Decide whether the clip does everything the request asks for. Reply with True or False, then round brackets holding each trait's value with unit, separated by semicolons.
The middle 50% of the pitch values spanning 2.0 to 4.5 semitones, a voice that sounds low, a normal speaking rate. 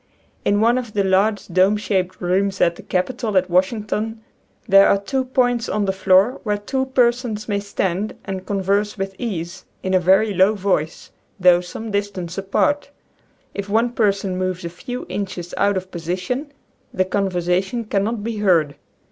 False (2.9 semitones; 200 Hz; 165 wpm)